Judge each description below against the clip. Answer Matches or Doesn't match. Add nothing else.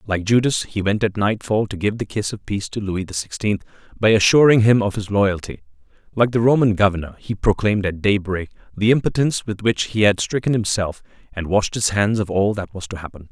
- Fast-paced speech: Matches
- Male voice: Matches